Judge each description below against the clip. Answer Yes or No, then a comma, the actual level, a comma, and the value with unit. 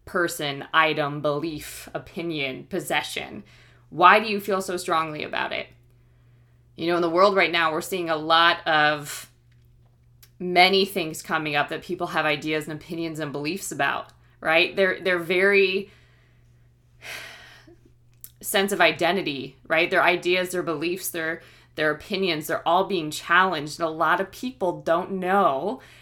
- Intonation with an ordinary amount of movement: Yes, average, 3.9 semitones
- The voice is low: No, medium, 160 Hz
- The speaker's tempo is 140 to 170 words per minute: Yes, average, 150 wpm